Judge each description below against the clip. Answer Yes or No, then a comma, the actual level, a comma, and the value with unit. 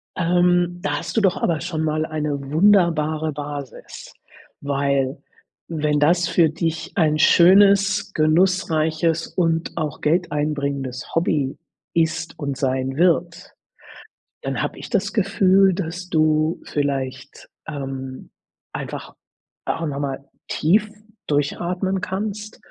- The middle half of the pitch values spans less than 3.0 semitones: No, average, 3.6 semitones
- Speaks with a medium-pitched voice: Yes, medium, 160 Hz